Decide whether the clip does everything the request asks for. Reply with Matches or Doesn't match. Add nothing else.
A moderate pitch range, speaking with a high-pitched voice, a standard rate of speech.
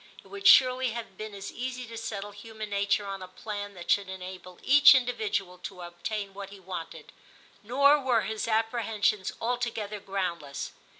Matches